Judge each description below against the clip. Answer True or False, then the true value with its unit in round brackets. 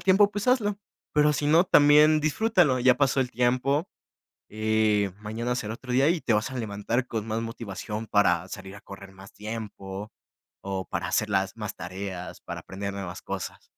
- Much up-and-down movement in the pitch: True (5.9 semitones)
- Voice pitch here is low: True (115 Hz)